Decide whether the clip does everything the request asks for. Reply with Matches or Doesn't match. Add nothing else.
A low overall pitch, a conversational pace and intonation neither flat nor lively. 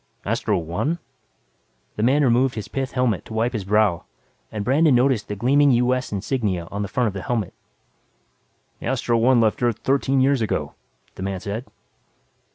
Matches